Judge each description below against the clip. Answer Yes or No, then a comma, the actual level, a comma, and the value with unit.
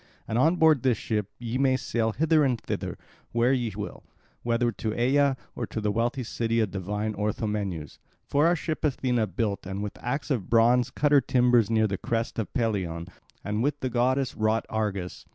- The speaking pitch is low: Yes, low, 115 Hz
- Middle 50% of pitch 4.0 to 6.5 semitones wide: No, average, 3.5 semitones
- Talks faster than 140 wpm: Yes, average, 190 wpm